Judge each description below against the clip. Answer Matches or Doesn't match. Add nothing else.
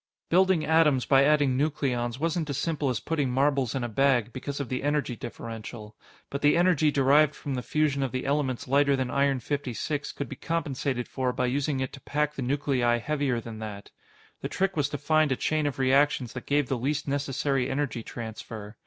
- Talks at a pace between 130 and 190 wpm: Doesn't match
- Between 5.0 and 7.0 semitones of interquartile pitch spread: Doesn't match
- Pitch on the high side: Doesn't match